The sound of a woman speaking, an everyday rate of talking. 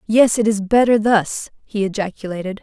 Yes: female; average, 160 wpm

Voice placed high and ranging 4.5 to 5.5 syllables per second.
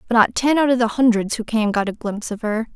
No: high, 225 Hz; 6.3 syllables/s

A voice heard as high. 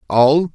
No: medium, 145 Hz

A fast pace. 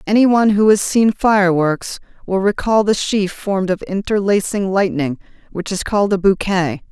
No: average, 165 wpm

